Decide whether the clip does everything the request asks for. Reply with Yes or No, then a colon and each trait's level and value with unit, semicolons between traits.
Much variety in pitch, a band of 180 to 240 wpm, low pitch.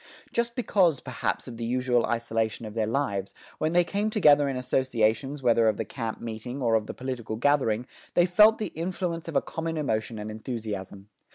Yes: wide, 6.4 semitones; average, 190 wpm; low, 125 Hz